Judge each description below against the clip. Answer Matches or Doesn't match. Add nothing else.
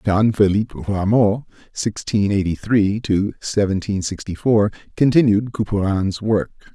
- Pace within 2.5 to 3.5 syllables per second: Matches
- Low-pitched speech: Matches